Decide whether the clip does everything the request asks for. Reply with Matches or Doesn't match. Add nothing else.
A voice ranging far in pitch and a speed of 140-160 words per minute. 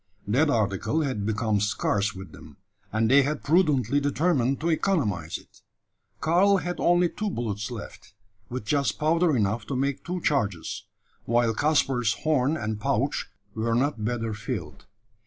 Matches